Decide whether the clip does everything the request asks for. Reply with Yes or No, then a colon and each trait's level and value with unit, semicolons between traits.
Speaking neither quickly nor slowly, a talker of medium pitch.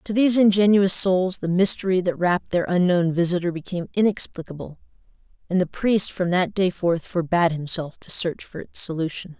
Yes: average, 170 wpm; medium, 180 Hz